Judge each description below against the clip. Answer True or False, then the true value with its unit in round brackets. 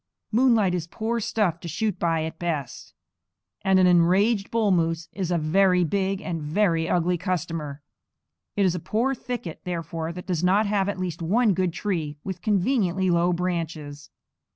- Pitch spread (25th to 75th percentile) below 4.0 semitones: True (3.2 semitones)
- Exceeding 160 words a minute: True (175 wpm)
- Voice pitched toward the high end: False (180 Hz)